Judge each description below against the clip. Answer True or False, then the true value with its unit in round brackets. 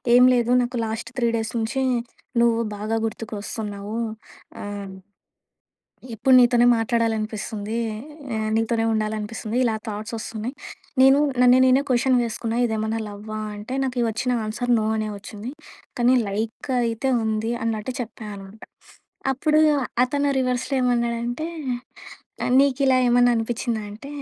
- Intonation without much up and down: True (2.3 semitones)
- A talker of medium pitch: False (225 Hz)